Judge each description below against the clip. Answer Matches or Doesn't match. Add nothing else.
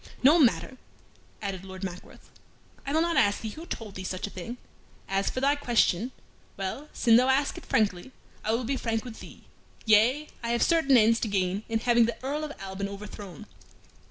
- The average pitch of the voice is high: Matches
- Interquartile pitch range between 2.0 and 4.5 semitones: Doesn't match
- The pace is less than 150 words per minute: Doesn't match